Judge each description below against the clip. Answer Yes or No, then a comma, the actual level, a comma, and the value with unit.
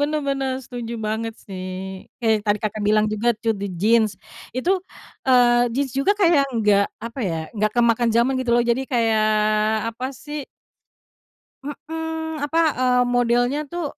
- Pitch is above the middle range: Yes, high, 240 Hz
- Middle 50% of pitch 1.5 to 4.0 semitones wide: Yes, average, 3.7 semitones